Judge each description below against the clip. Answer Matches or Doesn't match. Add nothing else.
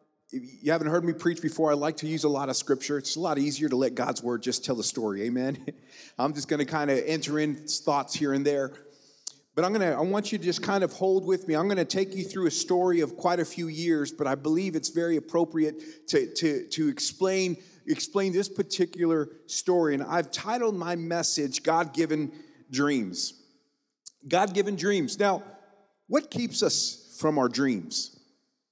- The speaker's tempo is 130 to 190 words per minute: Doesn't match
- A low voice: Doesn't match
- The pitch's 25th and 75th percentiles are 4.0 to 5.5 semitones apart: Matches